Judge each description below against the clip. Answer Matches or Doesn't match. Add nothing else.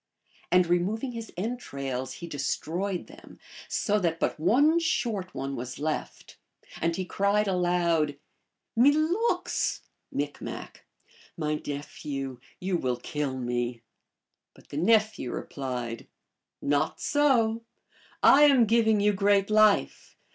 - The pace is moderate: Doesn't match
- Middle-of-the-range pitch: Matches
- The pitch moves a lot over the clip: Matches